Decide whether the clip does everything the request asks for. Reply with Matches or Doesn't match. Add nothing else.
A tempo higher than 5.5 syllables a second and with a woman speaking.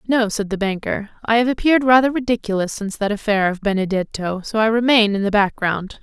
Matches